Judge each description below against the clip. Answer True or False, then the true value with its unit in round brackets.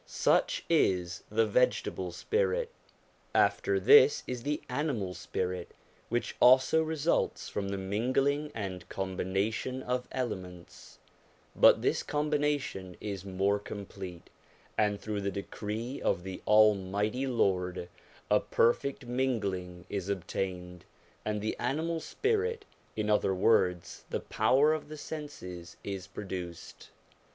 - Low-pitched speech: True (105 Hz)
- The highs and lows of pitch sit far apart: True (6.4 semitones)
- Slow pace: True (120 wpm)